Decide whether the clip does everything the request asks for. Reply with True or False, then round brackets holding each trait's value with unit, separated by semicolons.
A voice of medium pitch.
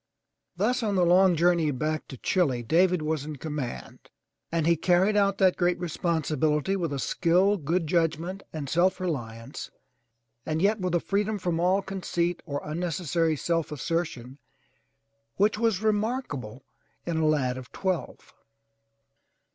True (170 Hz)